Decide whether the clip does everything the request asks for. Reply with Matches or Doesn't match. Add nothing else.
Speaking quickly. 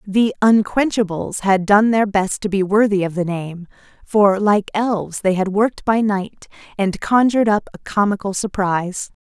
Doesn't match